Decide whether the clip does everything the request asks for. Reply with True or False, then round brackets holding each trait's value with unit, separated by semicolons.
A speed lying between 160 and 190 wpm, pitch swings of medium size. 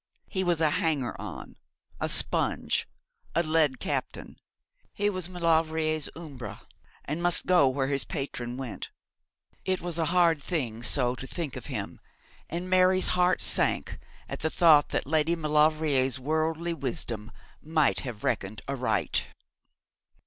False (140 wpm; 4.2 semitones)